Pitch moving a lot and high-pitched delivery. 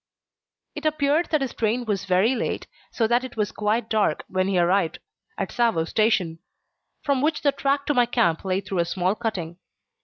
Yes: wide, 5.7 semitones; high, 220 Hz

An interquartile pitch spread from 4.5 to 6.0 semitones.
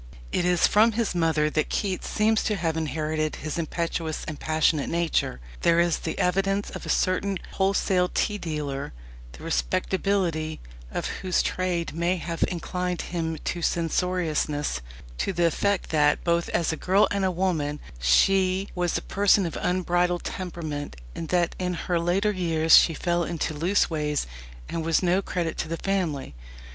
No: average, 2.7 semitones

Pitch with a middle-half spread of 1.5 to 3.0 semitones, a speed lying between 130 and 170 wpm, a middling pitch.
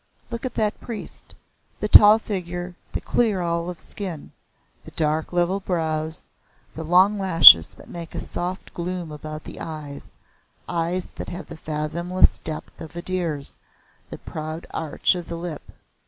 Yes: average, 2.7 semitones; average, 155 wpm; medium, 170 Hz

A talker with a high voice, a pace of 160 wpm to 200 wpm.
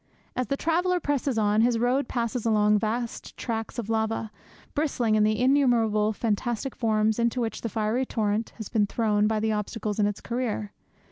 Yes: high, 225 Hz; average, 180 wpm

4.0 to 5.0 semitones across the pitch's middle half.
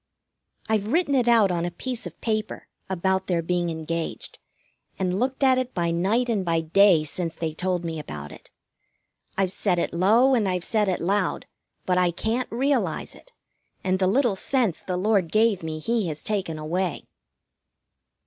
Yes: average, 4.7 semitones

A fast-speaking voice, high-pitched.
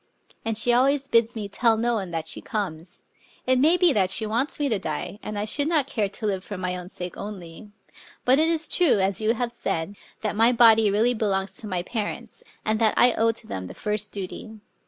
Yes: fast, 230 wpm; high, 215 Hz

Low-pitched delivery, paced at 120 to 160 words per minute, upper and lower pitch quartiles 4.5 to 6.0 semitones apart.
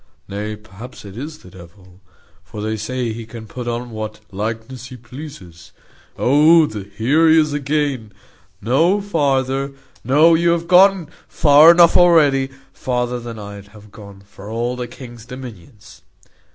Yes: low, 125 Hz; average, 150 wpm; wide, 5.5 semitones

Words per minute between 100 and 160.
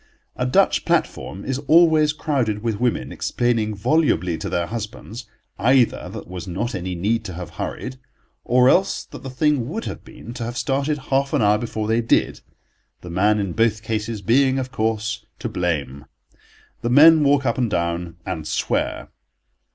No: average, 175 wpm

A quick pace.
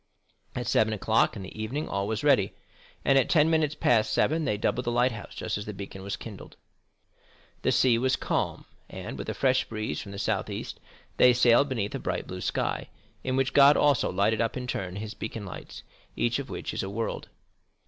Yes: fast, 210 wpm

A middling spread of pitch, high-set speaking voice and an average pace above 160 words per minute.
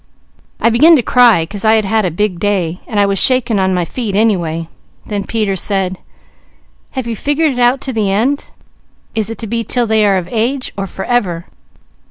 Yes: average, 3.8 semitones; high, 215 Hz; fast, 205 wpm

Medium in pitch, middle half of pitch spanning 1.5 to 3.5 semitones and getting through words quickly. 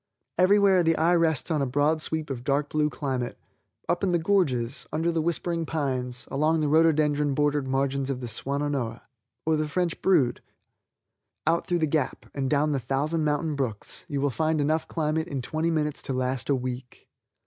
No: medium, 150 Hz; average, 3.0 semitones; average, 190 wpm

